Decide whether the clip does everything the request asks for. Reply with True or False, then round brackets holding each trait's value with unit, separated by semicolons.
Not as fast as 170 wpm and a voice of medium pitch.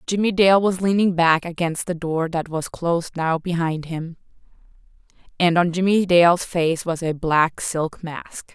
True (160 wpm; 170 Hz)